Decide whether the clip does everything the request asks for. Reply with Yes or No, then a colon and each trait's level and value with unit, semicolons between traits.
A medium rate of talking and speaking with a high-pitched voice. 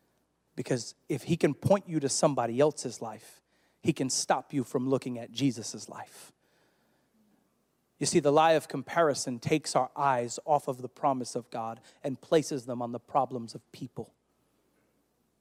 No: average, 165 wpm; low, 135 Hz